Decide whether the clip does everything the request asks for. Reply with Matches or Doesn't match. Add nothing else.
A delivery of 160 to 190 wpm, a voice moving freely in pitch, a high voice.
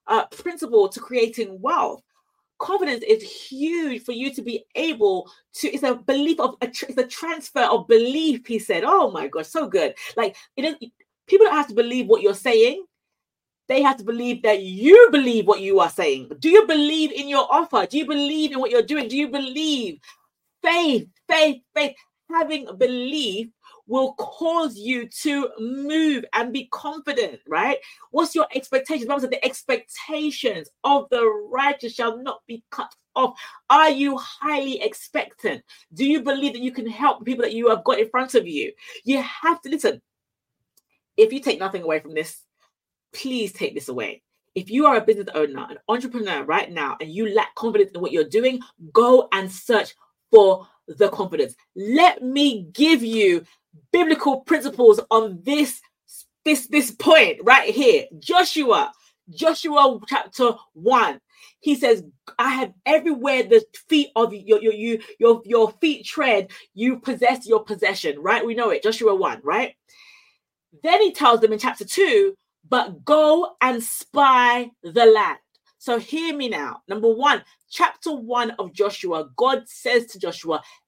Matches